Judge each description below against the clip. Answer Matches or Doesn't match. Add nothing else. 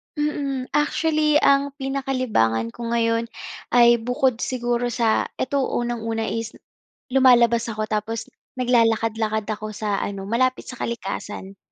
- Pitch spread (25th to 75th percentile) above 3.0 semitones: Doesn't match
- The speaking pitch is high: Matches